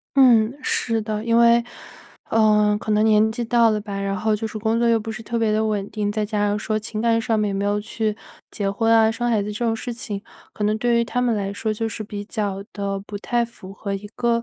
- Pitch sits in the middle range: No, high, 215 Hz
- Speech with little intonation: Yes, narrow, 1.8 semitones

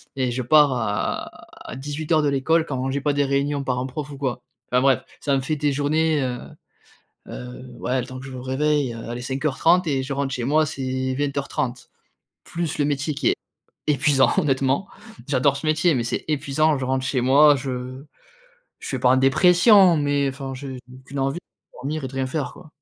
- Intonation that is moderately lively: No, narrow, 2.3 semitones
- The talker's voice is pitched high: No, low, 135 Hz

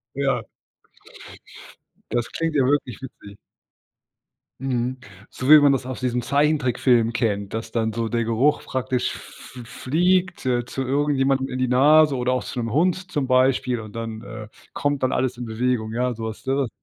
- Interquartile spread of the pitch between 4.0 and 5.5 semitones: No, average, 2.9 semitones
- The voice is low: Yes, low, 130 Hz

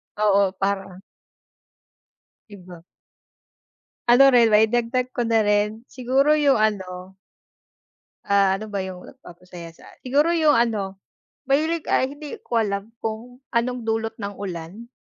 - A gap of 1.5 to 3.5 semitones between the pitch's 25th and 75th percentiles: No, average, 4.1 semitones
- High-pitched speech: Yes, high, 220 Hz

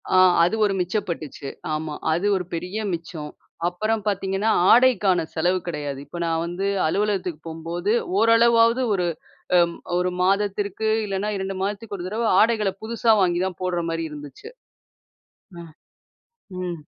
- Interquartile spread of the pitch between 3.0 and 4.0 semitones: Yes, average, 3.6 semitones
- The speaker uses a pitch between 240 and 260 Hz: No, high, 190 Hz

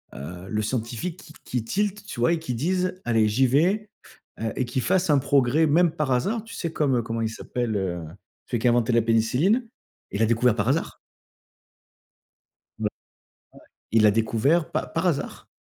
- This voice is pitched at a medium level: No, low, 125 Hz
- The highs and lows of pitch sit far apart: Yes, wide, 6.7 semitones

